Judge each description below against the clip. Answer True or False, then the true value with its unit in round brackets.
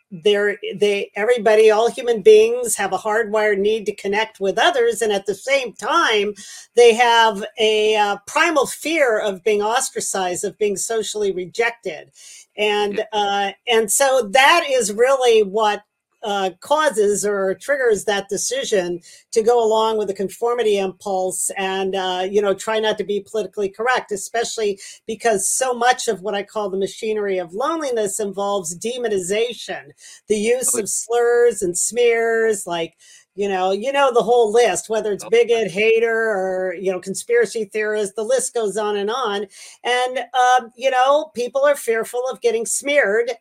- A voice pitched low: False (215 Hz)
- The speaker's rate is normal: True (160 wpm)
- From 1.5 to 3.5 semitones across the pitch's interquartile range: True (2.9 semitones)